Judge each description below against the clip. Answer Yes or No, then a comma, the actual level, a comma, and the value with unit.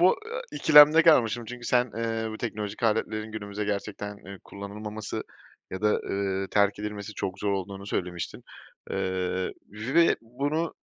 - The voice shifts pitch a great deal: No, average, 3.2 semitones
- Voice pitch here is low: Yes, low, 105 Hz